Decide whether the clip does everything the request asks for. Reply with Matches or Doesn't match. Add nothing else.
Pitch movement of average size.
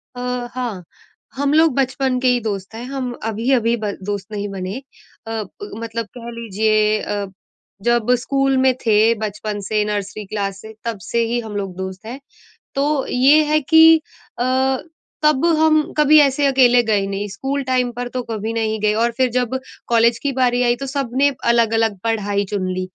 Matches